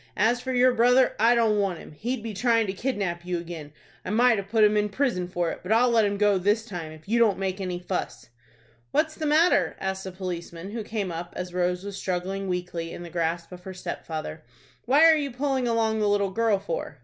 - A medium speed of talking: No, fast, 235 wpm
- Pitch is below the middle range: No, high, 200 Hz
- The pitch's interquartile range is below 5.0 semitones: Yes, average, 4.5 semitones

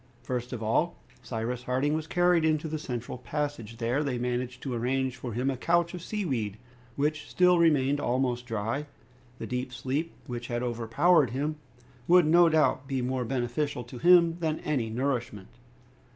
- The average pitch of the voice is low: Yes, low, 130 Hz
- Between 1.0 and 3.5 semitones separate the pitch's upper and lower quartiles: No, average, 4.1 semitones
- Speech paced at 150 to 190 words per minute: Yes, average, 170 wpm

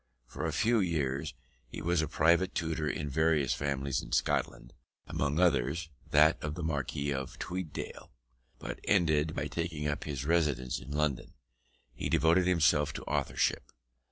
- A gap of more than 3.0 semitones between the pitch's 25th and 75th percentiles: No, average, 2.7 semitones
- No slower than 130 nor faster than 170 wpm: Yes, average, 155 wpm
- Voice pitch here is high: No, very low, 75 Hz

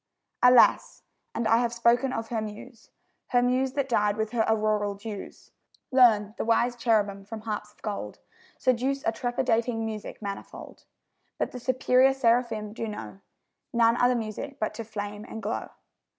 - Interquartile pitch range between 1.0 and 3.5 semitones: Yes, narrow, 2.5 semitones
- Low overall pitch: No, high, 230 Hz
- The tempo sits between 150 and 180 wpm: Yes, average, 160 wpm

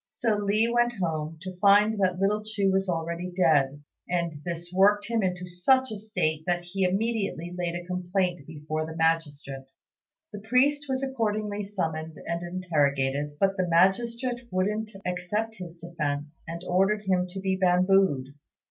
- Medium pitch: Yes, medium, 180 Hz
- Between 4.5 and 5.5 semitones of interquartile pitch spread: No, average, 3.8 semitones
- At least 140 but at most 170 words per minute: Yes, average, 155 wpm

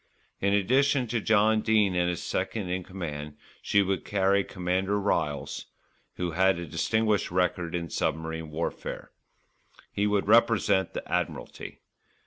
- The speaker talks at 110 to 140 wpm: Yes, slow, 135 wpm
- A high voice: No, very low, 95 Hz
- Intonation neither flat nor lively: Yes, average, 3.2 semitones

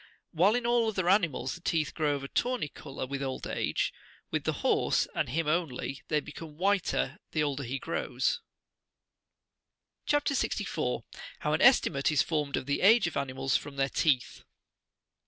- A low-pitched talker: No, medium, 150 Hz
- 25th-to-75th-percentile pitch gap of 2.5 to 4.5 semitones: No, average, 5.3 semitones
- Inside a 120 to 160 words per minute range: No, average, 170 wpm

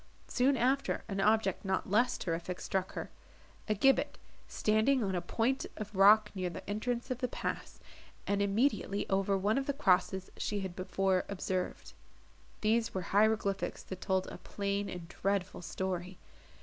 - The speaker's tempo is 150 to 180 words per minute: Yes, average, 155 wpm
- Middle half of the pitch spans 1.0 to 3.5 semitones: Yes, average, 2.7 semitones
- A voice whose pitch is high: Yes, high, 200 Hz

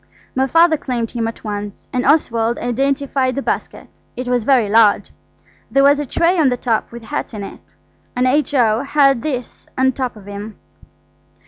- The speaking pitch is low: No, very high, 250 Hz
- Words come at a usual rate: Yes, average, 180 wpm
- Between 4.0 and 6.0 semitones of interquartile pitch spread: No, average, 3.5 semitones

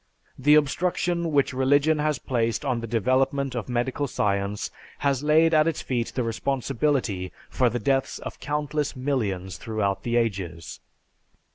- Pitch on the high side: No, low, 130 Hz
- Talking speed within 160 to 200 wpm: No, average, 145 wpm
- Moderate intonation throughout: Yes, average, 4.3 semitones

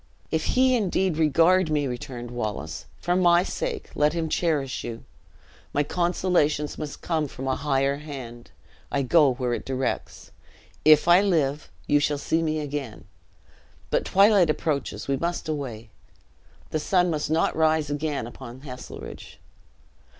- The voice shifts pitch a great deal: No, average, 3.8 semitones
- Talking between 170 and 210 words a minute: No, average, 145 wpm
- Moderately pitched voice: Yes, medium, 150 Hz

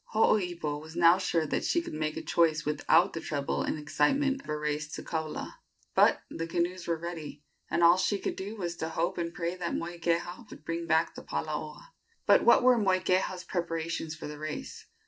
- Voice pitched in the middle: Yes, medium, 170 Hz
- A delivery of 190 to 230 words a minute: Yes, average, 200 wpm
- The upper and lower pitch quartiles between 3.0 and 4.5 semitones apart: No, narrow, 2.5 semitones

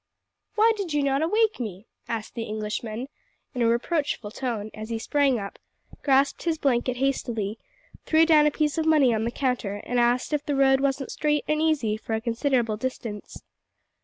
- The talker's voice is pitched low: No, very high, 260 Hz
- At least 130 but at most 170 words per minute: No, average, 185 wpm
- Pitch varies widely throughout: No, average, 4.8 semitones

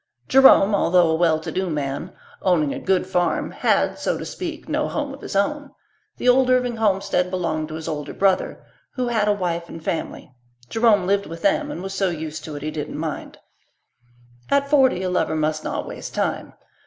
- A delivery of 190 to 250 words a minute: Yes, average, 200 wpm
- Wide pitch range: Yes, wide, 7.4 semitones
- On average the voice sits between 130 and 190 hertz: Yes, medium, 185 Hz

